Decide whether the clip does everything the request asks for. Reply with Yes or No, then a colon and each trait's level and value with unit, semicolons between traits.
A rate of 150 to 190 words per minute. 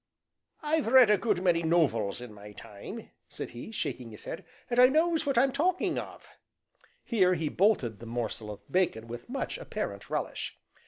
Yes: average, 180 wpm